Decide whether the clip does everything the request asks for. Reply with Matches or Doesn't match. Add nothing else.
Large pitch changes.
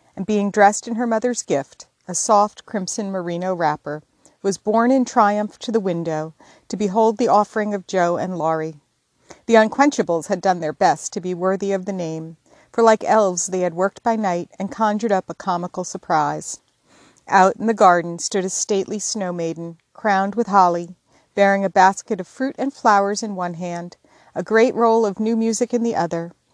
Doesn't match